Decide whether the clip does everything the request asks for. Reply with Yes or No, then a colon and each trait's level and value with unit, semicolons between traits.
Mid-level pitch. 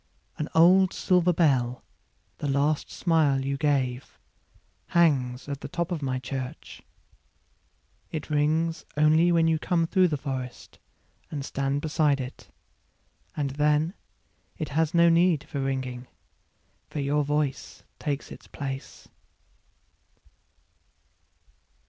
Yes: medium, 150 Hz